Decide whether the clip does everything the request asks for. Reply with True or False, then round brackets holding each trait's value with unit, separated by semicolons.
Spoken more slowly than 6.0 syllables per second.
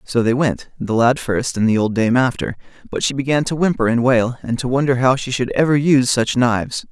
True (5.5 syllables/s)